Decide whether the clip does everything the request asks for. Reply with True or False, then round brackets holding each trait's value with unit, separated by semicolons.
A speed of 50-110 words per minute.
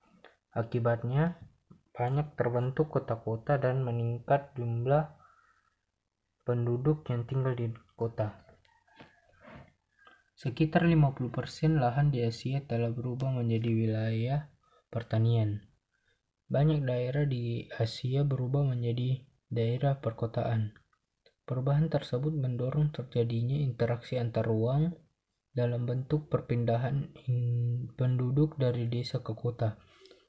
True (90 wpm)